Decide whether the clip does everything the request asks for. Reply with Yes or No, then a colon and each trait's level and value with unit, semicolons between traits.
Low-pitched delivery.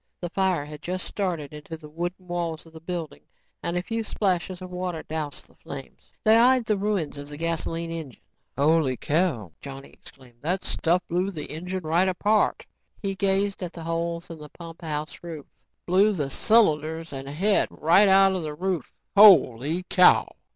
No: medium, 170 Hz